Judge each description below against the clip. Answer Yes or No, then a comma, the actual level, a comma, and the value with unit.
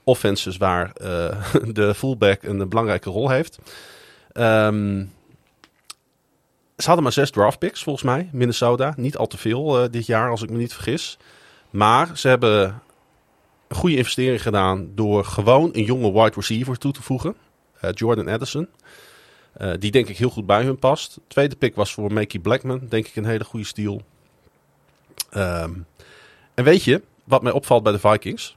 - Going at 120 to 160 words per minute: No, average, 170 wpm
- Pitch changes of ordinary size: Yes, average, 3.9 semitones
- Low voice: Yes, low, 110 Hz